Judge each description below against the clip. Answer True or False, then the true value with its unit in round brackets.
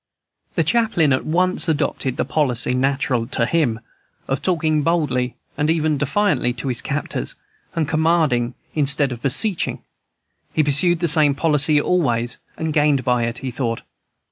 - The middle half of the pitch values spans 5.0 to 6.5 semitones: False (4.2 semitones)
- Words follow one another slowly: False (150 wpm)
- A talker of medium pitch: True (145 Hz)